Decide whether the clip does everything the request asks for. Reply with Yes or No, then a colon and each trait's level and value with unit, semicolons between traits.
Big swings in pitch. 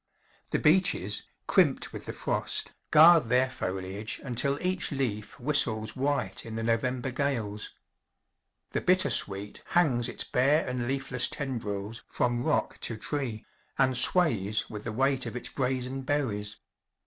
No: average, 4.3 semitones